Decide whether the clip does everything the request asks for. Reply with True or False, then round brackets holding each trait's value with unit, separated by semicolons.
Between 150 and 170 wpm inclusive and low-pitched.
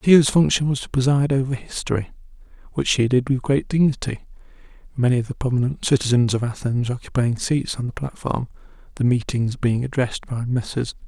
True (165 wpm; 125 Hz)